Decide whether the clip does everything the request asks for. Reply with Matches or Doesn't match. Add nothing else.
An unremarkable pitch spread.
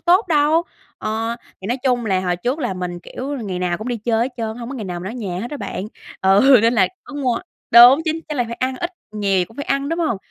Doesn't match